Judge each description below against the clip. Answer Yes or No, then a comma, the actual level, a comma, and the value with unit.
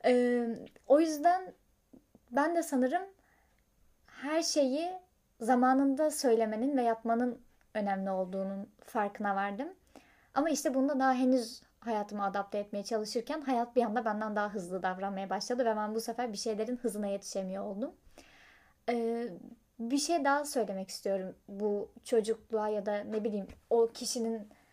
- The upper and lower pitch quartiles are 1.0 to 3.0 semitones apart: No, average, 4.0 semitones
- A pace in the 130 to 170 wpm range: Yes, average, 135 wpm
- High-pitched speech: Yes, high, 230 Hz